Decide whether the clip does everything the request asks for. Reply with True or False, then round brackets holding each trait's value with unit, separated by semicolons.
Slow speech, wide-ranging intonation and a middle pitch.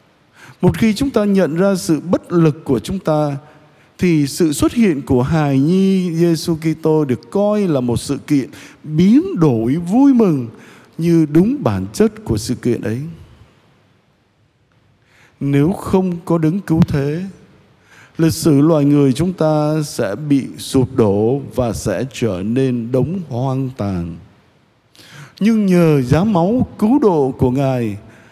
True (150 wpm; 5.7 semitones; 150 Hz)